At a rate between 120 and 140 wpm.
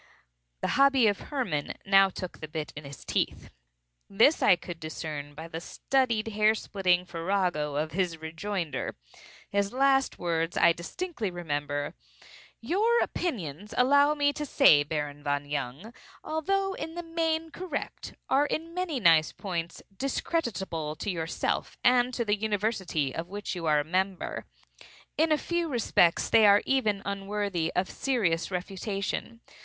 No: average, 150 wpm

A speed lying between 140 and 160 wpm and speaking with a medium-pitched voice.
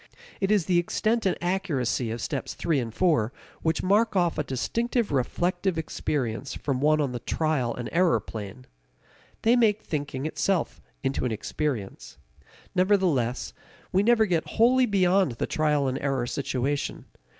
Yes: average, 150 wpm; medium, 155 Hz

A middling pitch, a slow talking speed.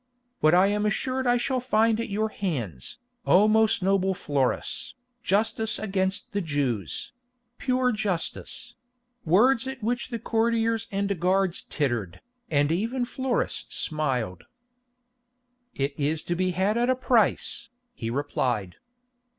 No: high, 200 Hz; slow, 125 wpm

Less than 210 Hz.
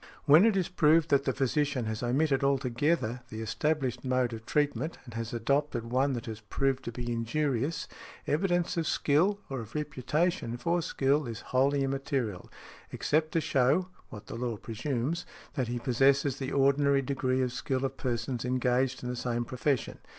Yes: low, 135 Hz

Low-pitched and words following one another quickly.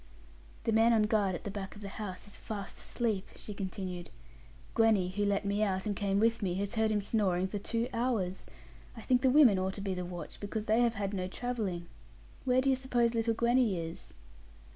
No: high, 205 Hz; fast, 215 wpm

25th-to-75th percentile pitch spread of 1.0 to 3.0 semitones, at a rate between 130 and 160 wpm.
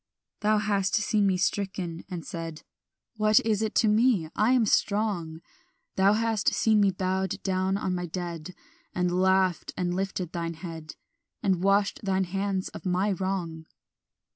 Yes: narrow, 2.6 semitones; average, 155 wpm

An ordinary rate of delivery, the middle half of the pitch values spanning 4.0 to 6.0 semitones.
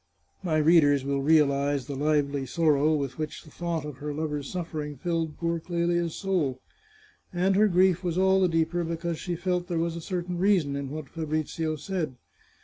No: average, 180 wpm; average, 3.0 semitones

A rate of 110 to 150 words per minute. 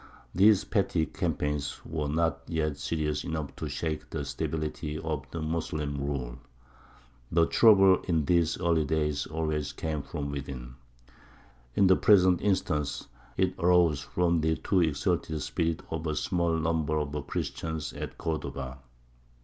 Yes: average, 140 wpm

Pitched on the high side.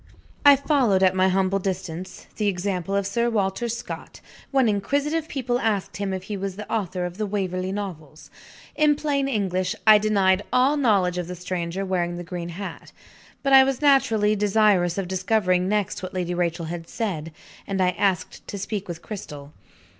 Yes: high, 195 Hz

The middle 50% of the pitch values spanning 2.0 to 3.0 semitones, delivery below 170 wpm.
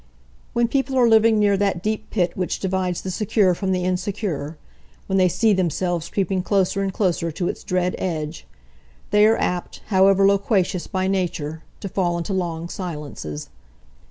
Yes: narrow, 2.6 semitones; average, 155 wpm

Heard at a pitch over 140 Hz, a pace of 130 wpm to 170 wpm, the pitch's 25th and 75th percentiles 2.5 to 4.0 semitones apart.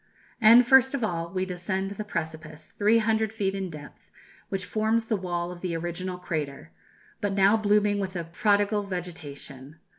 Yes: high, 190 Hz; average, 160 wpm; average, 3.7 semitones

